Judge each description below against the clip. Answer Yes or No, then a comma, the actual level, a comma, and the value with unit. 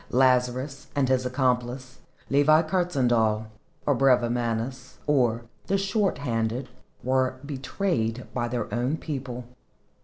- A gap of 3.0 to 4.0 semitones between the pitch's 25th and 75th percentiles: No, narrow, 2.6 semitones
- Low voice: Yes, low, 130 Hz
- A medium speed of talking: No, slow, 110 wpm